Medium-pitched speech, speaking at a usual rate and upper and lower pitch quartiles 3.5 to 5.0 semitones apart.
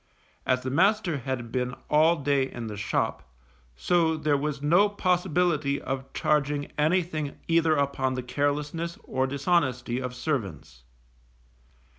No: medium, 145 Hz; slow, 130 wpm; average, 3.9 semitones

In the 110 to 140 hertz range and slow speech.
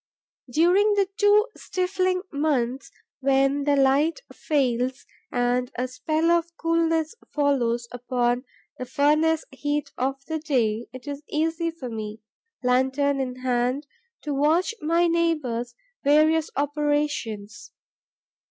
No: very high, 285 Hz; slow, 115 wpm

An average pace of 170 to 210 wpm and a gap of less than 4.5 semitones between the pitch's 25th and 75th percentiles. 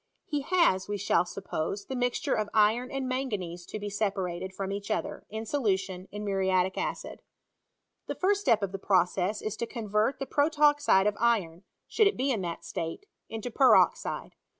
No: average, 175 wpm; average, 5.1 semitones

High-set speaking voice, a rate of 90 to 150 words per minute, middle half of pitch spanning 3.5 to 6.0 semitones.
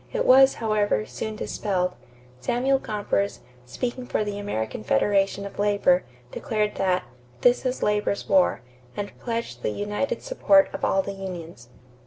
Yes: high, 205 Hz; average, 145 wpm; average, 4.0 semitones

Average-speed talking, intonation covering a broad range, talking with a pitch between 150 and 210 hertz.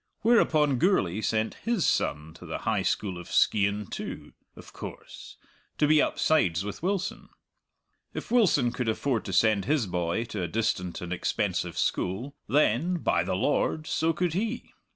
No: average, 160 wpm; wide, 9.0 semitones; low, 115 Hz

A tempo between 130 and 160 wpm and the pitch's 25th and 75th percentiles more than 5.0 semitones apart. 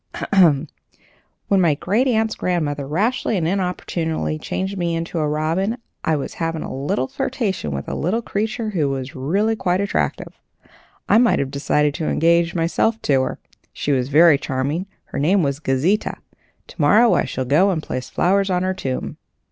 No: average, 175 wpm; wide, 5.4 semitones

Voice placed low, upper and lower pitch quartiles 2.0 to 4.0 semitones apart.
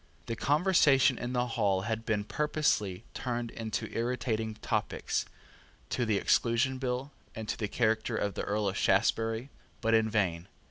Yes: low, 115 Hz; average, 2.8 semitones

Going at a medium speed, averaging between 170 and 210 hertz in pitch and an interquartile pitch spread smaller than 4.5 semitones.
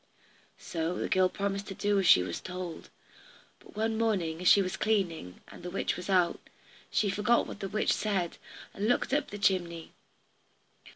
Yes: average, 180 wpm; high, 190 Hz; average, 2.9 semitones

